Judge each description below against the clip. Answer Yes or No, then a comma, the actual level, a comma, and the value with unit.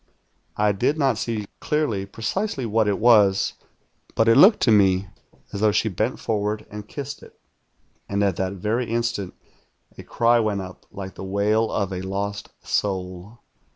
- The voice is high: No, low, 105 Hz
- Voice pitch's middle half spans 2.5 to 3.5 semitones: Yes, average, 2.9 semitones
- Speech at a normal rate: Yes, average, 165 wpm